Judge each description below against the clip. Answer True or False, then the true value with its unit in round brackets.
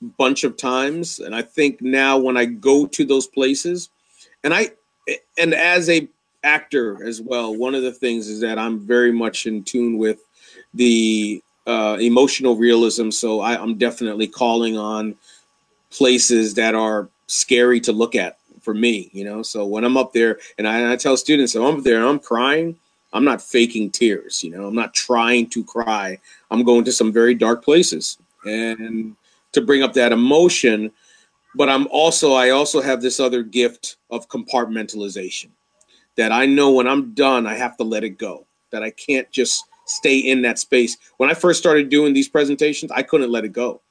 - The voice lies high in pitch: False (120 Hz)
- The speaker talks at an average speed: True (190 wpm)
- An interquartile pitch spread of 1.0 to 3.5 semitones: True (3.2 semitones)